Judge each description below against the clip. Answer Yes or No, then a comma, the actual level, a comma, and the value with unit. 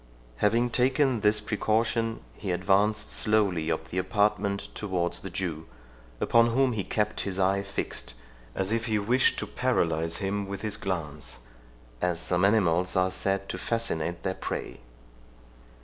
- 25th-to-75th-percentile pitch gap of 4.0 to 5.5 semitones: No, average, 3.1 semitones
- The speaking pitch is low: Yes, low, 100 Hz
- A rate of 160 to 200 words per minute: No, average, 150 wpm